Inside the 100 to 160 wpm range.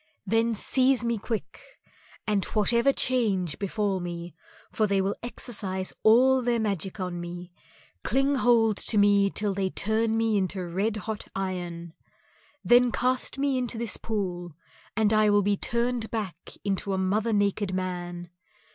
Yes: average, 150 wpm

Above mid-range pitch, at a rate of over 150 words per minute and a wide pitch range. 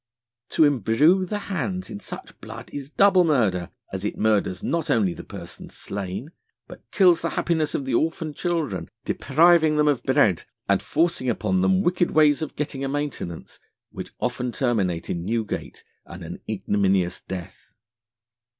No: medium, 140 Hz; average, 160 wpm; wide, 8.6 semitones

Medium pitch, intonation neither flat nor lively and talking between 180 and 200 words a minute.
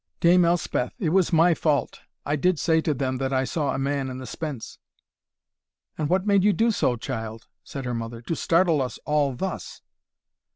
Yes: medium, 150 Hz; average, 4.8 semitones; average, 195 wpm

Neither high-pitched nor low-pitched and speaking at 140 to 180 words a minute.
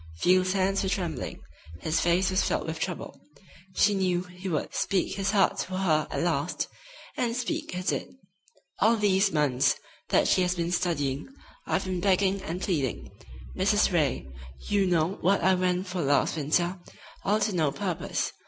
Yes: medium, 180 Hz; average, 170 wpm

